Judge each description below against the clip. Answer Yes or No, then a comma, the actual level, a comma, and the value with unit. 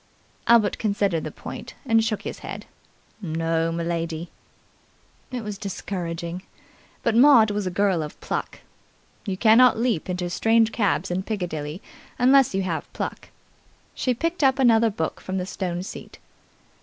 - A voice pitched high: Yes, high, 195 Hz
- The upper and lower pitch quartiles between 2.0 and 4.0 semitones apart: No, average, 4.7 semitones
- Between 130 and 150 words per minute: Yes, average, 145 wpm